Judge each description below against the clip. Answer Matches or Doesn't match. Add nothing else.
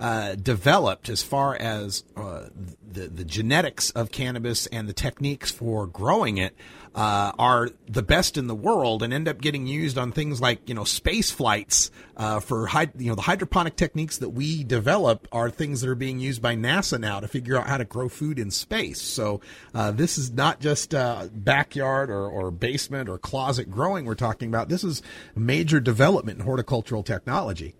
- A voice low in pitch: Matches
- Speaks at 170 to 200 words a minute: Matches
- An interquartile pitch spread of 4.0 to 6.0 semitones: Matches